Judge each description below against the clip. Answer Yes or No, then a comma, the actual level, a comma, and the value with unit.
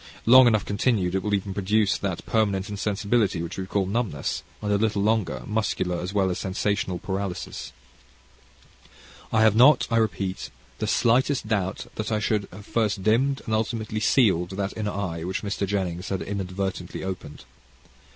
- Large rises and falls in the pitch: No, narrow, 2.6 semitones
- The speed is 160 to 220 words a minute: Yes, average, 165 wpm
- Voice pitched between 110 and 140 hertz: No, low, 100 Hz